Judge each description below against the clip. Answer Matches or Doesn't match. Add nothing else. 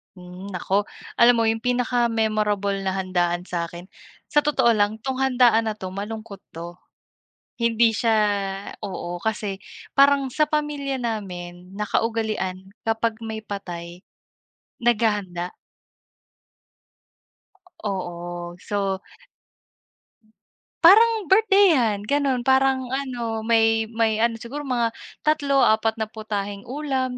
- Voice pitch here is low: Doesn't match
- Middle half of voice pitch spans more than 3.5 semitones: Matches